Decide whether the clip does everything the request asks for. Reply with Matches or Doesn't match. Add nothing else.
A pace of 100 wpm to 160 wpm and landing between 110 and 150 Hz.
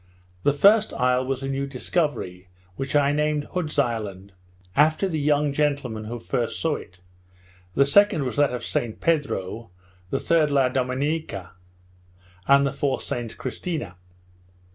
Matches